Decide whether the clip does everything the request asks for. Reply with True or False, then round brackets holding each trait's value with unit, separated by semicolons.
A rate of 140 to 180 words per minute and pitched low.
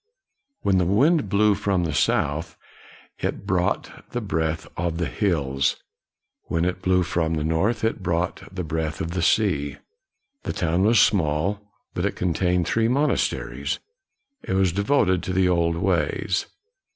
True (150 wpm; 90 Hz)